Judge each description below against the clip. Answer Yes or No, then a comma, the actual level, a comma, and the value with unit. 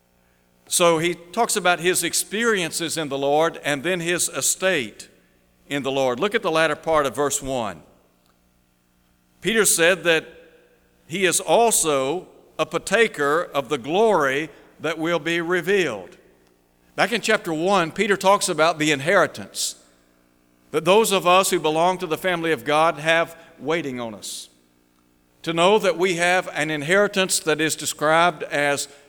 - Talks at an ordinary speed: Yes, average, 155 wpm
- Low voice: No, medium, 160 Hz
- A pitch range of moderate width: No, wide, 6.3 semitones